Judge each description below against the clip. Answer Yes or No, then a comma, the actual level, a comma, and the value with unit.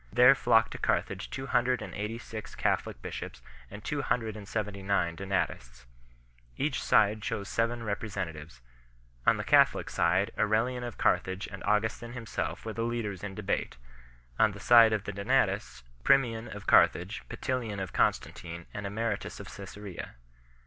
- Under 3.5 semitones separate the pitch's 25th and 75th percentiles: Yes, average, 3.0 semitones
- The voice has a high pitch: No, low, 105 Hz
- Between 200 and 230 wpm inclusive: No, average, 165 wpm